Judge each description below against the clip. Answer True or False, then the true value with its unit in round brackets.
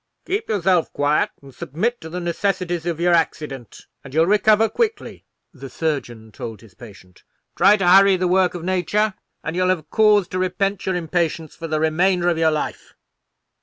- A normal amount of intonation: True (3.5 semitones)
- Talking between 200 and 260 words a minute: False (180 wpm)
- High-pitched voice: False (175 Hz)